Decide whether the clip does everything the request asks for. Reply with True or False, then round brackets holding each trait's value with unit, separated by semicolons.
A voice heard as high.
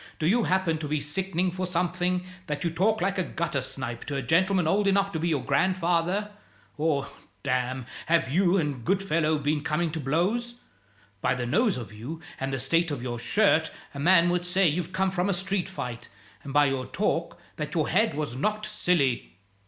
False (165 Hz)